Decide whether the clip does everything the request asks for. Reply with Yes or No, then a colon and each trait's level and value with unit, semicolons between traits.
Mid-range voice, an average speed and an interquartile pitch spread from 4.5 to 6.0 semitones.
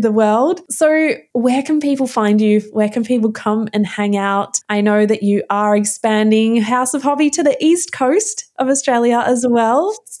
No: high, 235 Hz; average, 195 wpm; average, 5.1 semitones